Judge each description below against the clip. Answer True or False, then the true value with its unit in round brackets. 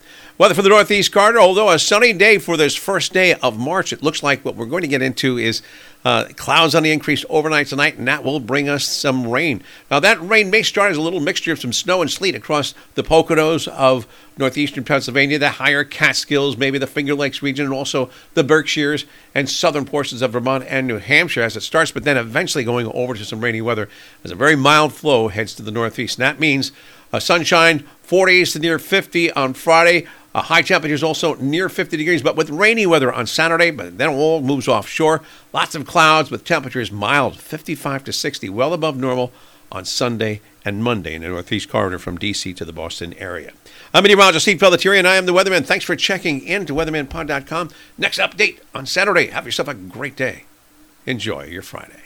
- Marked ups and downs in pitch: False (4.4 semitones)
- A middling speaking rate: False (210 wpm)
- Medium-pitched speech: True (145 Hz)